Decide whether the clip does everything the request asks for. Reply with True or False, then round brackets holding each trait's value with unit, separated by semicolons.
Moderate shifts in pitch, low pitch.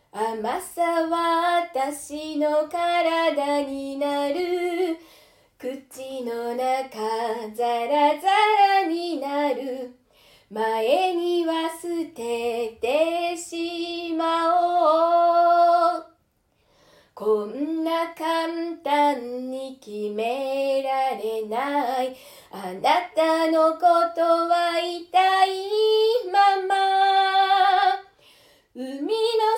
False (4.7 semitones; 325 Hz)